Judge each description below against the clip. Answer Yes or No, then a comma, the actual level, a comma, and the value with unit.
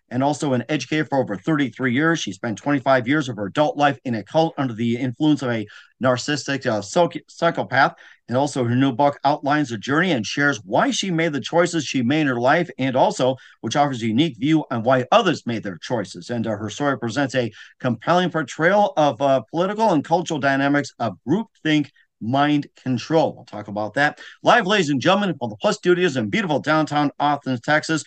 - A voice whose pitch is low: No, medium, 145 Hz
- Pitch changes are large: No, average, 3.8 semitones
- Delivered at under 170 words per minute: No, fast, 205 wpm